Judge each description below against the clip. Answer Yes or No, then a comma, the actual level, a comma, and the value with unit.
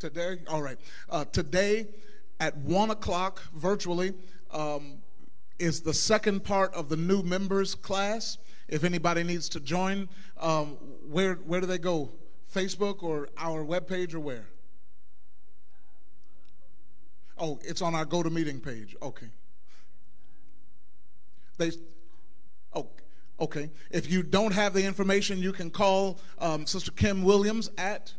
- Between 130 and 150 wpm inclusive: Yes, slow, 135 wpm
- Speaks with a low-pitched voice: No, medium, 175 Hz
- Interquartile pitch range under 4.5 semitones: Yes, average, 3.8 semitones